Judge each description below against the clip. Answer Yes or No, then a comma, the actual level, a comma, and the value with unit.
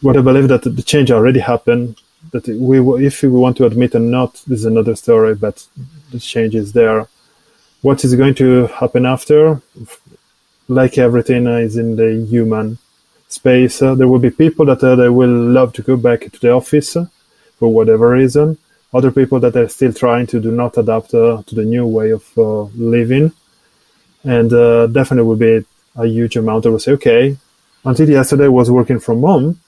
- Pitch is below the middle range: Yes, low, 125 Hz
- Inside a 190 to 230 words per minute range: Yes, average, 200 wpm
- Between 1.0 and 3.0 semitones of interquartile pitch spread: Yes, average, 2.7 semitones